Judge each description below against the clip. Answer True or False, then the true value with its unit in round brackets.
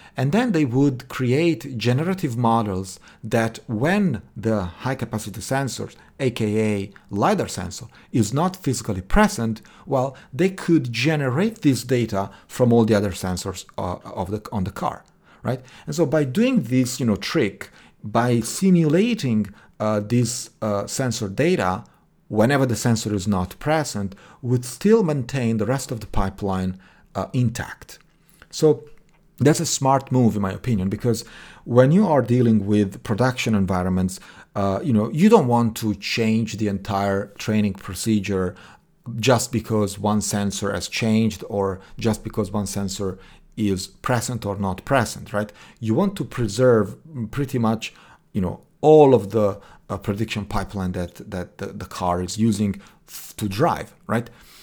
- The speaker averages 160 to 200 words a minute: False (150 wpm)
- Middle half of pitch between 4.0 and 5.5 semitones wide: True (4.7 semitones)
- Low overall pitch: True (115 Hz)